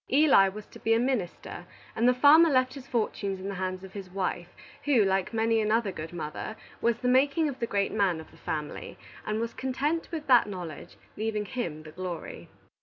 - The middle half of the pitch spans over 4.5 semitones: Yes, wide, 5.4 semitones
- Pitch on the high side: Yes, high, 215 Hz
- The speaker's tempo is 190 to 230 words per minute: Yes, fast, 205 wpm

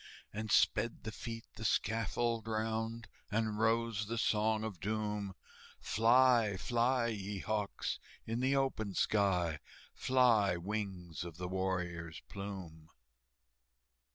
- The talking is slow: Yes, slow, 115 wpm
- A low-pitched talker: Yes, low, 110 Hz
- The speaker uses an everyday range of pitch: Yes, average, 3.0 semitones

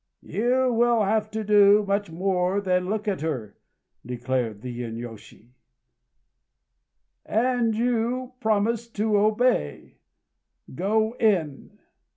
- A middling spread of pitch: No, wide, 5.8 semitones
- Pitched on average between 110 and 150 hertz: No, high, 205 Hz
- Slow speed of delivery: Yes, slow, 105 wpm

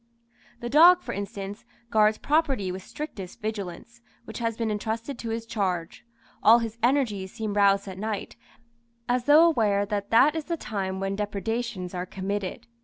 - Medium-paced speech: Yes, average, 165 wpm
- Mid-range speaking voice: No, high, 215 Hz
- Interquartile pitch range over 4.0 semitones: No, average, 3.2 semitones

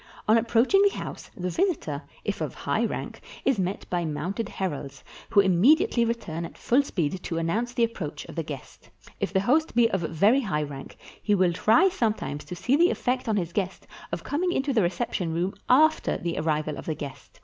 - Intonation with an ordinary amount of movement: No, wide, 6.7 semitones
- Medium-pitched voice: No, high, 195 Hz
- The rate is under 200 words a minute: No, fast, 205 wpm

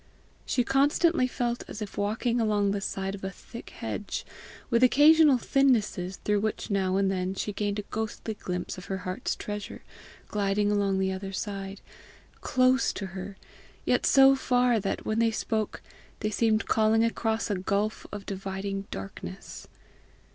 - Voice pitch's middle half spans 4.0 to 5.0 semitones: No, average, 3.0 semitones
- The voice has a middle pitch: No, high, 210 Hz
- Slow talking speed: No, average, 160 wpm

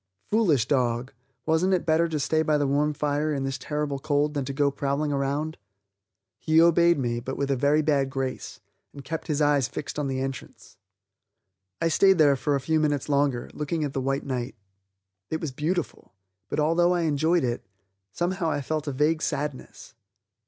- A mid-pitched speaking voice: Yes, medium, 145 Hz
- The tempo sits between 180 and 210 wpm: Yes, average, 190 wpm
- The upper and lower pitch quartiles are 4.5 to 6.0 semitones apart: No, narrow, 2.5 semitones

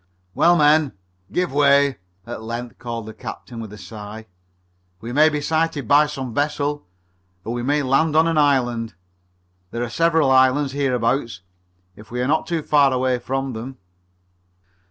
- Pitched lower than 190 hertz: Yes, low, 135 Hz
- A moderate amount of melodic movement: Yes, average, 3.8 semitones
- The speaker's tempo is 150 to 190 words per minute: Yes, average, 160 wpm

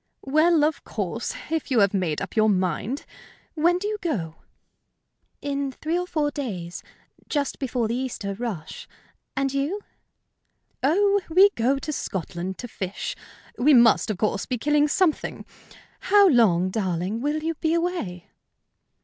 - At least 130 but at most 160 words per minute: Yes, average, 150 wpm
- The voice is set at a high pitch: Yes, very high, 265 Hz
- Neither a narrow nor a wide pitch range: No, wide, 7.9 semitones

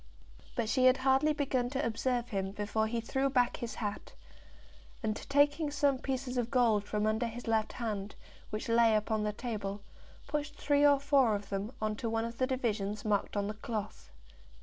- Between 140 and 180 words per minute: No, average, 190 wpm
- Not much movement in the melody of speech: No, average, 3.7 semitones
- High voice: Yes, high, 230 Hz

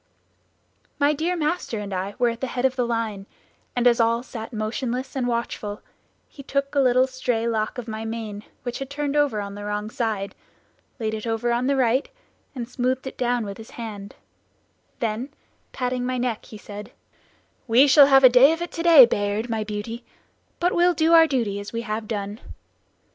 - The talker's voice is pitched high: Yes, high, 240 Hz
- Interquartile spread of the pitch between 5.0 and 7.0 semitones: No, average, 3.4 semitones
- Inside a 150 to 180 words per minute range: No, average, 195 wpm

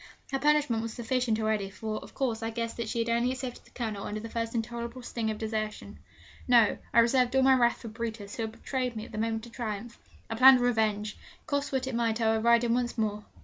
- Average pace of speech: No, fast, 240 wpm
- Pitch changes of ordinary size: No, narrow, 1.9 semitones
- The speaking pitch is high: Yes, high, 230 Hz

